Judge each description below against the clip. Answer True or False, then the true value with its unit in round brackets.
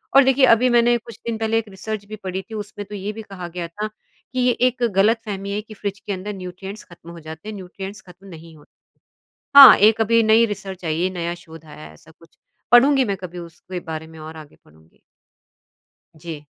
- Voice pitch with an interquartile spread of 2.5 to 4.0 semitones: False (4.4 semitones)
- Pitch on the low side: False (195 Hz)